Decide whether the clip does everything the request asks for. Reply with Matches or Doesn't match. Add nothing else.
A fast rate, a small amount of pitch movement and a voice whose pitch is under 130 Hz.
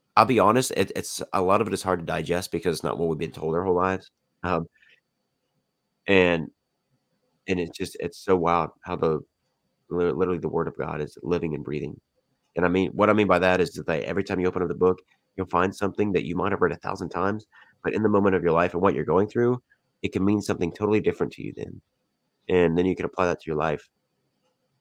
Matches